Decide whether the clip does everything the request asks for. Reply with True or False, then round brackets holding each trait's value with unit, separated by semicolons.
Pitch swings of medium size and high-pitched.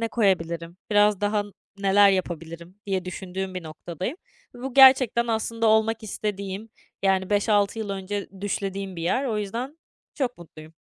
True (3.1 semitones; 200 Hz)